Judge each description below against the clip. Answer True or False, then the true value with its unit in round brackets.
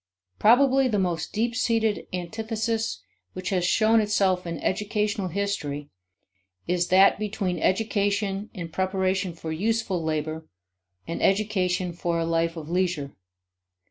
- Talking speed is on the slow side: True (125 wpm)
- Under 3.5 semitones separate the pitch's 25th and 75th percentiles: False (3.8 semitones)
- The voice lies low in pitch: False (190 Hz)